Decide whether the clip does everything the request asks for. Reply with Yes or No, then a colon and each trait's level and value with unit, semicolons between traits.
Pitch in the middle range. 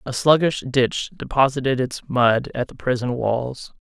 No: low, 130 Hz